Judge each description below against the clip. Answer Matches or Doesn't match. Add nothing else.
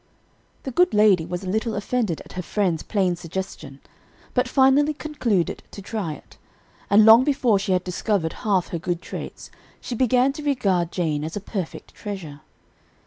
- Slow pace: Doesn't match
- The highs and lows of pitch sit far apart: Matches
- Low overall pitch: Doesn't match